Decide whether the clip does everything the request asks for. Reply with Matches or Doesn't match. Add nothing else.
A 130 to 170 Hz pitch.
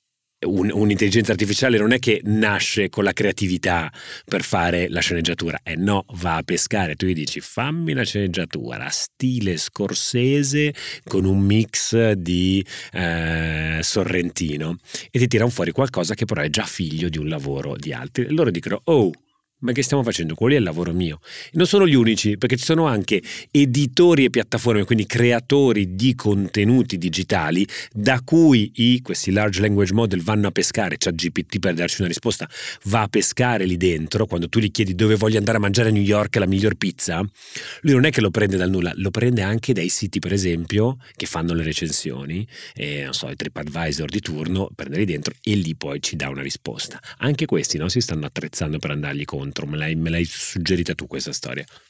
Doesn't match